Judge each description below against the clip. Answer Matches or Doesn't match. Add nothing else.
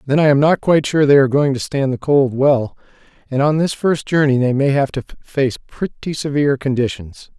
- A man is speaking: Matches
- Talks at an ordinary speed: Doesn't match